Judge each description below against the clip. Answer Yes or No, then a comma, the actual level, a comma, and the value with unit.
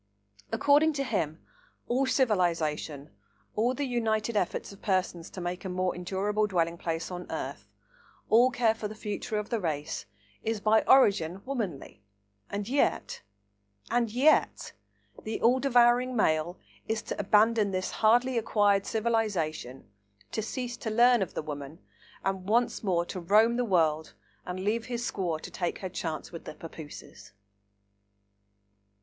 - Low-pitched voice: No, high, 205 Hz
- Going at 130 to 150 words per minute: Yes, average, 145 wpm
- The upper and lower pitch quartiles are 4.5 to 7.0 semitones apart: Yes, wide, 5.5 semitones